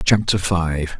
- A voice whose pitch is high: No, very low, 90 Hz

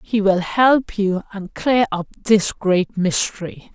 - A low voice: No, high, 200 Hz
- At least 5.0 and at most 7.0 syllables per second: No, 3.5 syllables/s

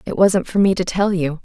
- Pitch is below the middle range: No, medium, 185 Hz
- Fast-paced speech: Yes, fast, 290 wpm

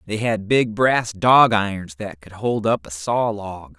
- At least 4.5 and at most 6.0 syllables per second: No, 3.9 syllables/s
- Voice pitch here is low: Yes, low, 105 Hz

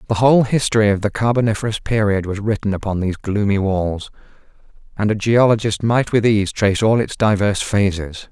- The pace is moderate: Yes, average, 175 wpm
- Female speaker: No, male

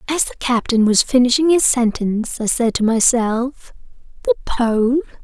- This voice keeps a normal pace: Yes, average, 150 wpm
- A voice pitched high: Yes, high, 245 Hz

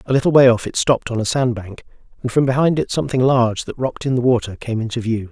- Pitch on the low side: Yes, low, 120 Hz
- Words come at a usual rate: No, fast, 270 wpm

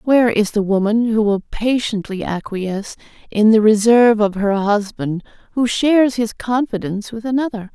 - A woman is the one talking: Yes, female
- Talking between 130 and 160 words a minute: Yes, average, 155 wpm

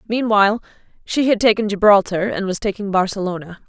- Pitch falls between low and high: No, high, 205 Hz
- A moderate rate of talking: Yes, average, 145 wpm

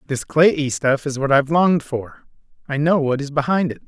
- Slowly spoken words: No, average, 200 wpm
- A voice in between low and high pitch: Yes, medium, 145 Hz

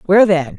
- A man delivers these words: No, female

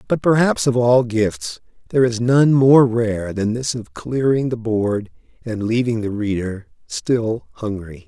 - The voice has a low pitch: Yes, low, 115 Hz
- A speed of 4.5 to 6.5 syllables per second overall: No, 4.0 syllables/s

